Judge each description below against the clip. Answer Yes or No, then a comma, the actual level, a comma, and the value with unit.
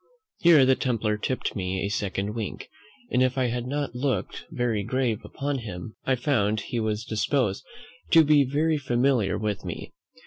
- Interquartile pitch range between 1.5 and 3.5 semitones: No, average, 4.3 semitones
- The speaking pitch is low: Yes, low, 120 Hz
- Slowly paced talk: No, average, 170 wpm